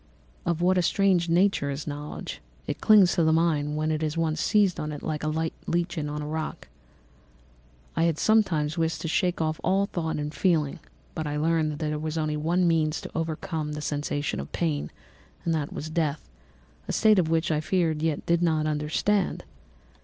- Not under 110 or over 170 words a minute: No, average, 185 wpm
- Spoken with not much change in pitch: Yes, narrow, 2.2 semitones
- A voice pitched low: No, medium, 160 Hz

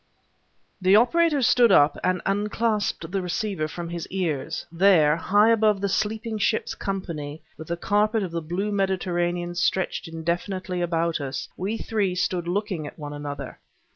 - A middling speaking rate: Yes, average, 155 wpm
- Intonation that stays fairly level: No, average, 3.7 semitones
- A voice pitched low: No, medium, 185 Hz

